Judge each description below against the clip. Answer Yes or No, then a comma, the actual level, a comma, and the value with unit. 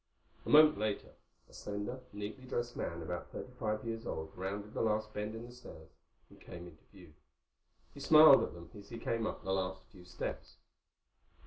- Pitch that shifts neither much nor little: Yes, average, 4.1 semitones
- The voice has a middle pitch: No, low, 105 Hz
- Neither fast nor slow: Yes, average, 190 wpm